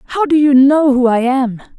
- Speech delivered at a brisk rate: Yes, fast, 235 wpm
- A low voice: No, very high, 270 Hz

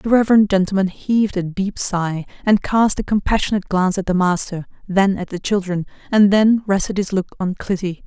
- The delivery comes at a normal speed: Yes, average, 195 wpm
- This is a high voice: Yes, high, 195 Hz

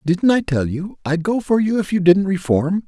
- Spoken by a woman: No, male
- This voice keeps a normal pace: No, fast, 250 wpm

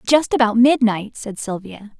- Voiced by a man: No, female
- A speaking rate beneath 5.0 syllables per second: Yes, 4.5 syllables/s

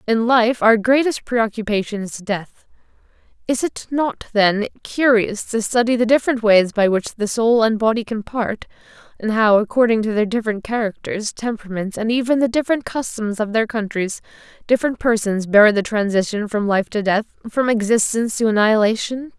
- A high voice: Yes, high, 225 Hz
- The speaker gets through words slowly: No, average, 165 wpm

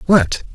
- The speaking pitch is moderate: Yes, medium, 150 Hz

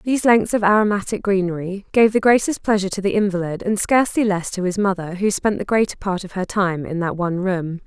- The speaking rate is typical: No, fast, 230 wpm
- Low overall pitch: No, high, 195 Hz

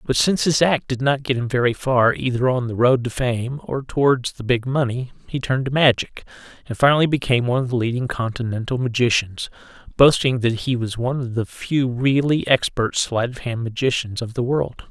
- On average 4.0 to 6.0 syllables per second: Yes, 5.5 syllables/s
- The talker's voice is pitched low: Yes, low, 125 Hz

